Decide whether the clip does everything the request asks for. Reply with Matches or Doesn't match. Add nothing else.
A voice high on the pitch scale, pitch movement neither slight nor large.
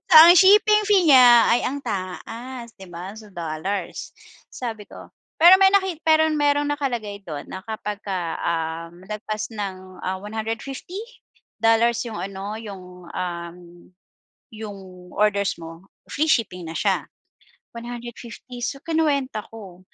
Doesn't match